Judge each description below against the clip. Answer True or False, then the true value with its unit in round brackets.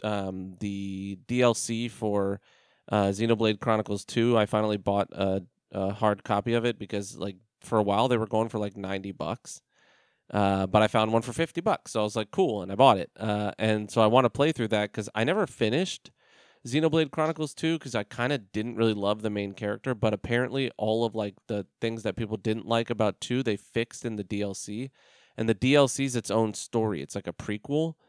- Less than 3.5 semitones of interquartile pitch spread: True (2.7 semitones)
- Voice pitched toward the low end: True (110 Hz)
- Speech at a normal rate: False (215 wpm)